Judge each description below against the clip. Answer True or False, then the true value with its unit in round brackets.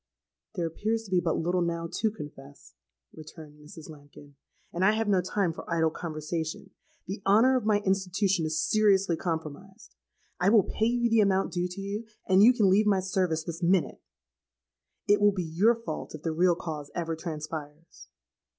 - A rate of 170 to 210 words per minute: True (180 wpm)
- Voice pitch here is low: False (180 Hz)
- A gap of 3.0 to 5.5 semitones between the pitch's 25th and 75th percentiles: True (4.2 semitones)